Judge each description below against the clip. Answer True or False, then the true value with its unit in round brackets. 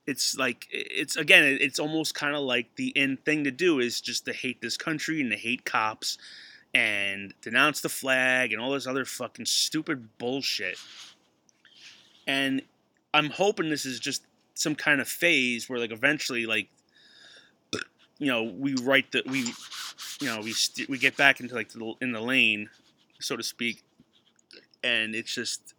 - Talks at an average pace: True (175 wpm)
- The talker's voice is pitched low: True (130 Hz)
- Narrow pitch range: False (3.3 semitones)